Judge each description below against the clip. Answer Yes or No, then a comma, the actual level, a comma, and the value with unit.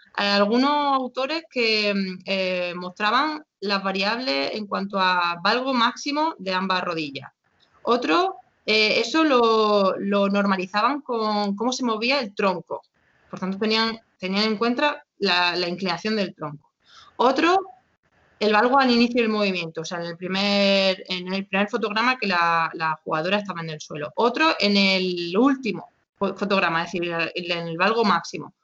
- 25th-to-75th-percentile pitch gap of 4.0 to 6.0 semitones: Yes, average, 4.5 semitones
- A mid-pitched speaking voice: No, high, 200 Hz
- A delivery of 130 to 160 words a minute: Yes, average, 155 wpm